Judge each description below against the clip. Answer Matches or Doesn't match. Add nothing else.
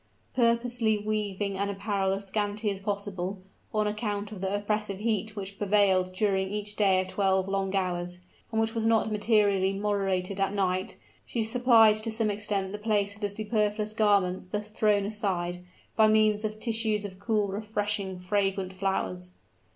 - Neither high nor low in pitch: Doesn't match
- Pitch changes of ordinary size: Doesn't match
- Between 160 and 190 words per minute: Matches